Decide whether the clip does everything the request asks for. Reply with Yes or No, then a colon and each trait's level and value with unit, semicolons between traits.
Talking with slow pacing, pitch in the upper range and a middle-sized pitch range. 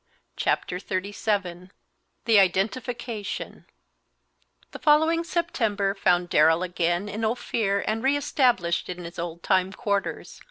Yes: slow, 115 wpm; high, 200 Hz; average, 4.5 semitones